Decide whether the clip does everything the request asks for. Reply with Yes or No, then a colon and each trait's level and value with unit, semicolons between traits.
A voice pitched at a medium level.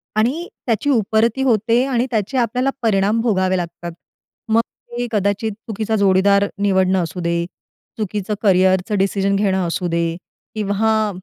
No: high, 205 Hz